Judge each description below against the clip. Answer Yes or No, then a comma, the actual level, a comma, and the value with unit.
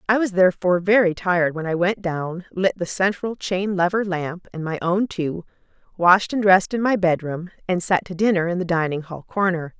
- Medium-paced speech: No, fast, 210 wpm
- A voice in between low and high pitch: Yes, medium, 180 Hz